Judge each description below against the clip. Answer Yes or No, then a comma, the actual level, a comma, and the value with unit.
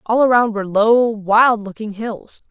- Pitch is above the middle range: Yes, high, 220 Hz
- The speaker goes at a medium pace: Yes, average, 170 wpm